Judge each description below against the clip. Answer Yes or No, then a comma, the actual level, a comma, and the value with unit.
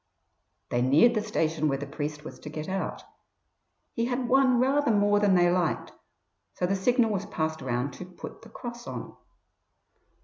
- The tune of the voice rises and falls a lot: Yes, wide, 7.4 semitones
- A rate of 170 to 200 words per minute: Yes, average, 175 wpm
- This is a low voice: No, high, 190 Hz